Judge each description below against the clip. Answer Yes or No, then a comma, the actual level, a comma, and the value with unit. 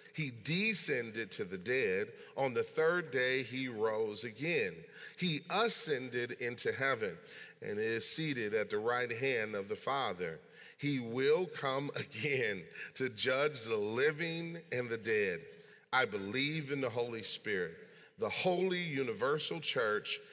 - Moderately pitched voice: Yes, medium, 155 Hz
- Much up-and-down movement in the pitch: Yes, wide, 8.1 semitones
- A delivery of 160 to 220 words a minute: No, average, 140 wpm